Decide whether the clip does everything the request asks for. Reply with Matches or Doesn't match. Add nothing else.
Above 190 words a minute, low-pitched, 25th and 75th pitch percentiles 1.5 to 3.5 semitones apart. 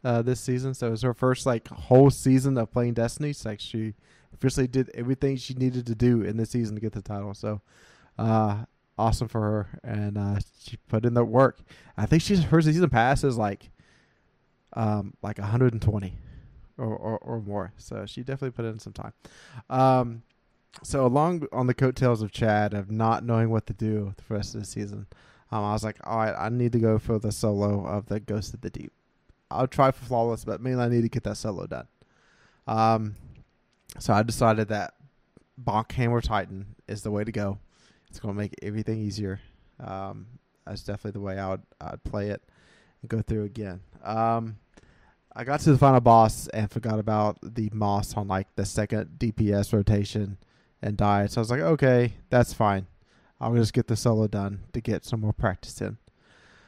Matches